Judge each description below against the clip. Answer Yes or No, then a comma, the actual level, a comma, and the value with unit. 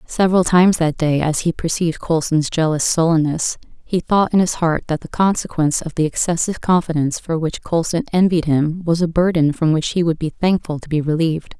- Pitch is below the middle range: No, medium, 165 Hz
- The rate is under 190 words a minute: No, average, 200 wpm